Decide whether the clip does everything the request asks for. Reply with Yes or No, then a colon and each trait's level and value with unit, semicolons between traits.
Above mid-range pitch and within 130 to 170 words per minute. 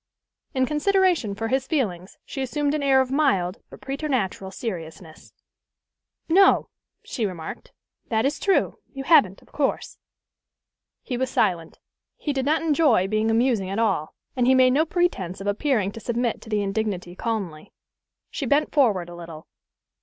Yes: high, 230 Hz; average, 160 wpm